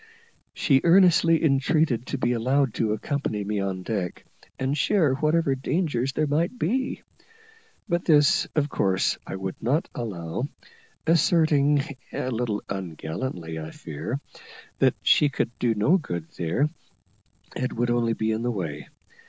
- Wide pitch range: Yes, wide, 6.7 semitones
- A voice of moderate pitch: No, low, 130 Hz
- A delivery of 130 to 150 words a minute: Yes, average, 145 wpm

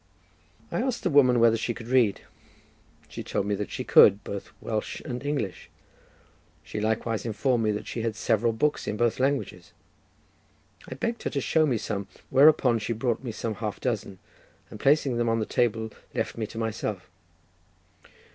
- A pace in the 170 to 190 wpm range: Yes, average, 175 wpm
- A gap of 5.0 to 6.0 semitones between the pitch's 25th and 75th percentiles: No, average, 3.3 semitones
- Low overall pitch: Yes, low, 115 Hz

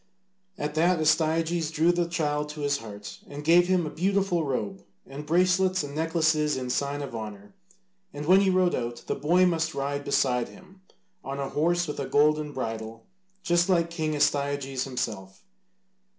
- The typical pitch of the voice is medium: Yes, medium, 150 Hz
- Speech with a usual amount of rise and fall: Yes, average, 3.8 semitones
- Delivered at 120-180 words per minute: Yes, average, 170 wpm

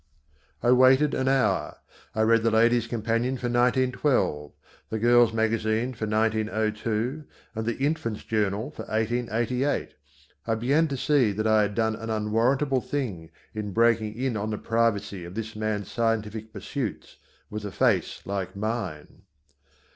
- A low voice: Yes, low, 110 Hz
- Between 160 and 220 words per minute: No, average, 145 wpm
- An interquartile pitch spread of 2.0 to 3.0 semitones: Yes, narrow, 2.4 semitones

